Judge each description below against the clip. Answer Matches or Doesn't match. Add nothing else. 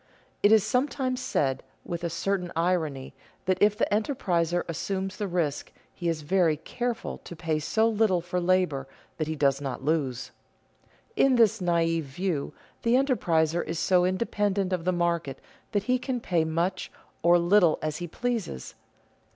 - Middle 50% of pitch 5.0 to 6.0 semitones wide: Doesn't match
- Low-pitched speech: Doesn't match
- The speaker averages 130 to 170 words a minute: Matches